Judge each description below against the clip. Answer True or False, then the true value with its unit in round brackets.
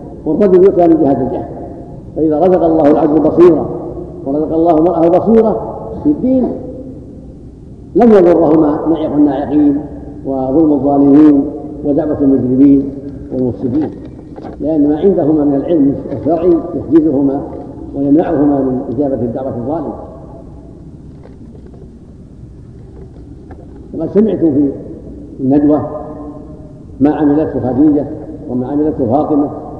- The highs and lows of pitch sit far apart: False (2.6 semitones)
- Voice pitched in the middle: True (150 Hz)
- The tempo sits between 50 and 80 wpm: False (95 wpm)